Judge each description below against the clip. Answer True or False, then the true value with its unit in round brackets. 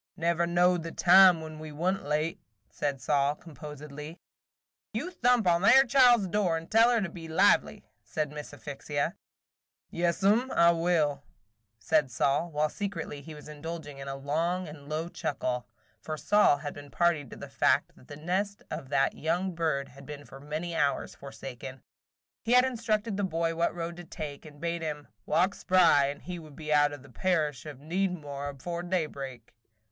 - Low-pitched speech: False (160 Hz)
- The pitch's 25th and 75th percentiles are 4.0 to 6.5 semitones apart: False (3.5 semitones)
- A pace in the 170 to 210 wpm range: True (185 wpm)